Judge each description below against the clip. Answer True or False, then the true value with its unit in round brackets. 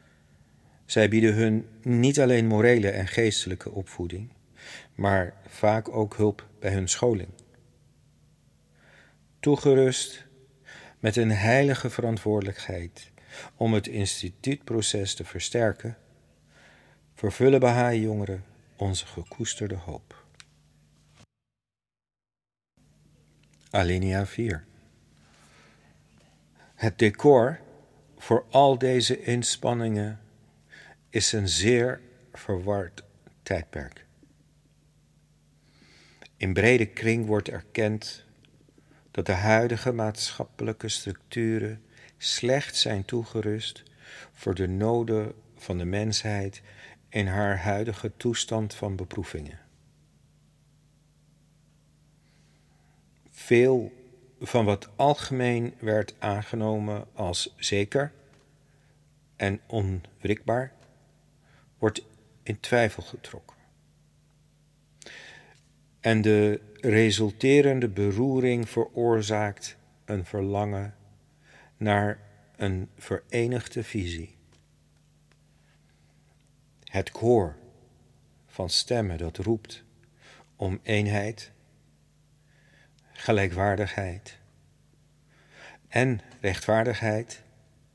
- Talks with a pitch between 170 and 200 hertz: False (110 Hz)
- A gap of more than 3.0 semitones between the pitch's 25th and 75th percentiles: True (3.5 semitones)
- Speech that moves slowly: True (70 wpm)